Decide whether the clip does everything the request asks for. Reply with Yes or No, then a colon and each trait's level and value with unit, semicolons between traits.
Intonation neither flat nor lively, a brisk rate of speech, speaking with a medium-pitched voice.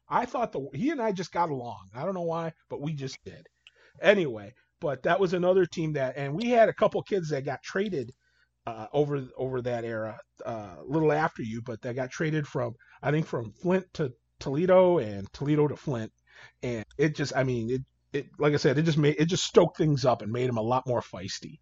Yes: average, 5.0 semitones; fast, 230 wpm; medium, 145 Hz